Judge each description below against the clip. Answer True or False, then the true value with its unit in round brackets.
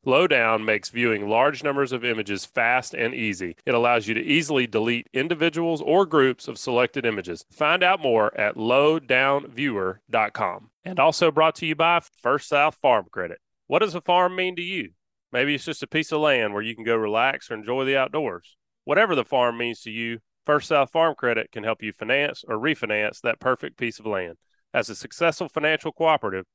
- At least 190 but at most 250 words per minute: True (195 wpm)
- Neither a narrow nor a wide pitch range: False (5.9 semitones)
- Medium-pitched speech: False (130 Hz)